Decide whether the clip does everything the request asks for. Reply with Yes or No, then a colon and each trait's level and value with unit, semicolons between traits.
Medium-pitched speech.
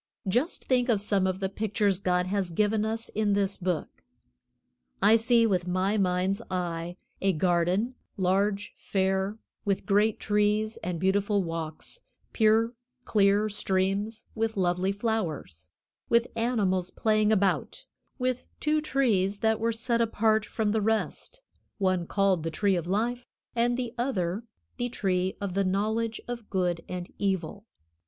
No: high, 200 Hz